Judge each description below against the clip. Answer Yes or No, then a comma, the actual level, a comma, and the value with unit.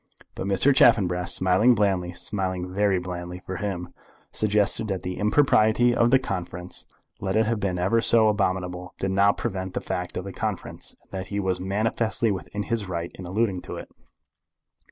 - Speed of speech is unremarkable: Yes, average, 175 wpm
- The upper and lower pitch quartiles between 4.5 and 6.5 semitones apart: No, average, 2.8 semitones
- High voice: No, very low, 95 Hz